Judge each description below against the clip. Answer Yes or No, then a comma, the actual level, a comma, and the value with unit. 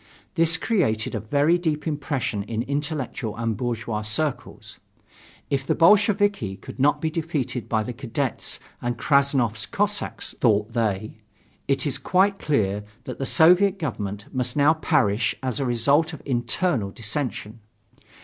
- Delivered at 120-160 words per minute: Yes, average, 140 wpm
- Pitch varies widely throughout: Yes, wide, 5.8 semitones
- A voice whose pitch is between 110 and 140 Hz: Yes, low, 135 Hz